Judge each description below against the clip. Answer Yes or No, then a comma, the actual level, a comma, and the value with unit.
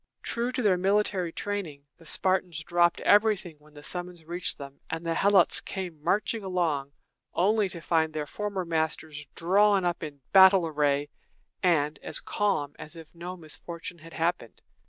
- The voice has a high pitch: No, medium, 170 Hz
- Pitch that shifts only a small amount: No, average, 3.5 semitones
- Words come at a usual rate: Yes, average, 160 wpm